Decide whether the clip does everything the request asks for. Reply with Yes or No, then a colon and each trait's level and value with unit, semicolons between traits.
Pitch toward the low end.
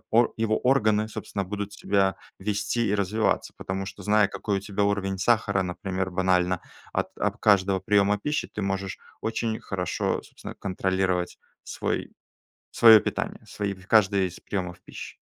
Yes: low, 100 Hz